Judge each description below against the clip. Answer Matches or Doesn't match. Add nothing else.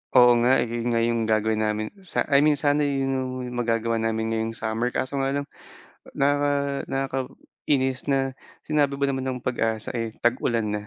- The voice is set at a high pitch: Doesn't match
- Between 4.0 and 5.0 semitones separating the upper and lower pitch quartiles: Doesn't match